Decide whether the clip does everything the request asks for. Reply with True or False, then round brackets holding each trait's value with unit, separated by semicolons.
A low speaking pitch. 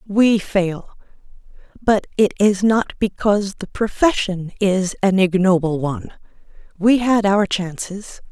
False (200 Hz)